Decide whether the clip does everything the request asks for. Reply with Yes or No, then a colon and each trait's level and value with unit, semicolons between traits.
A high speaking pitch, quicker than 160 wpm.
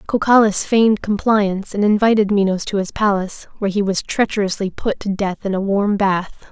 Yes: high, 200 Hz; average, 185 wpm